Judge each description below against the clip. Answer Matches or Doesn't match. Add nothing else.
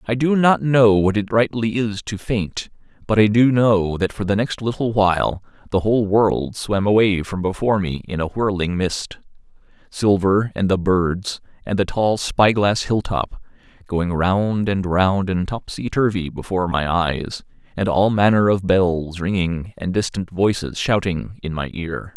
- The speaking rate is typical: Matches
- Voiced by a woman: Doesn't match